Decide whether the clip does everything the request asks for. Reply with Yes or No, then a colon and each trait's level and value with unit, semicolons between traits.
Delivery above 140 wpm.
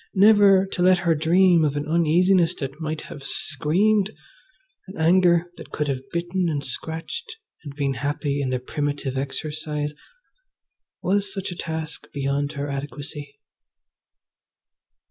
No: slow, 135 wpm